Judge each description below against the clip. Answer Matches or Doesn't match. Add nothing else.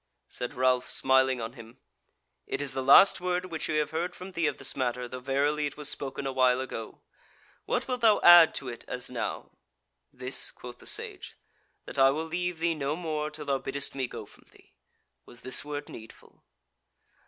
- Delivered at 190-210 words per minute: Matches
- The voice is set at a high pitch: Doesn't match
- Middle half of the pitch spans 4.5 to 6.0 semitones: Doesn't match